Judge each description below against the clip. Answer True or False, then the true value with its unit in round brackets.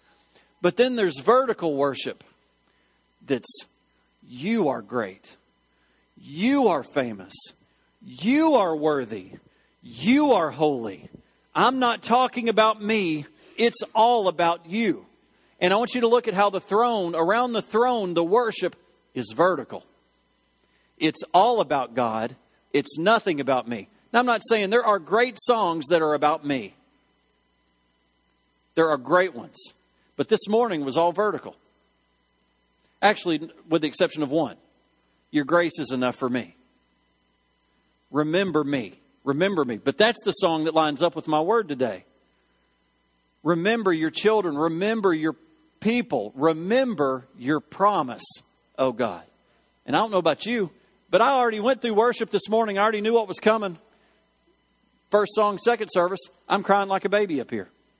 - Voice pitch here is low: False (175 Hz)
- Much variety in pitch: True (7.5 semitones)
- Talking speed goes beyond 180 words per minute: False (150 wpm)